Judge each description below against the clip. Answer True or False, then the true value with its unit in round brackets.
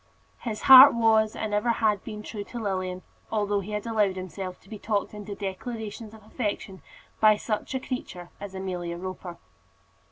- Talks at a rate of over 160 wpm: True (170 wpm)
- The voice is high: True (210 Hz)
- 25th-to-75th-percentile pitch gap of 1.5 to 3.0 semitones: True (2.6 semitones)